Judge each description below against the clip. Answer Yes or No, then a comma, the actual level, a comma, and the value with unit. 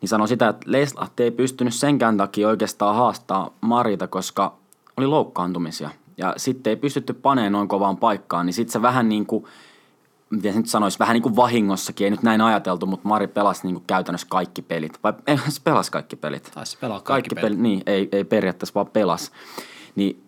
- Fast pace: Yes, fast, 190 wpm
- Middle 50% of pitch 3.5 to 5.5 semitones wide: Yes, average, 3.8 semitones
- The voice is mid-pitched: No, low, 110 Hz